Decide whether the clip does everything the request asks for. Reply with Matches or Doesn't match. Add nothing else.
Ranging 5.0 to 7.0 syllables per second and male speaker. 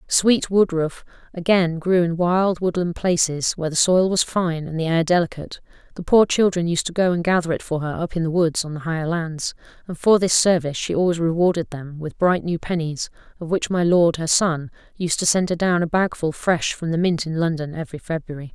Doesn't match